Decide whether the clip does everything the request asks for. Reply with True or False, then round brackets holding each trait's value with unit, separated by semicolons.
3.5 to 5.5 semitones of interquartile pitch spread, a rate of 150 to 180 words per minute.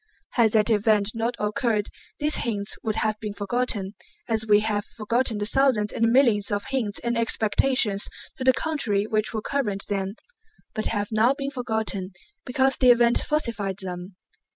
False (3.0 semitones; 165 wpm)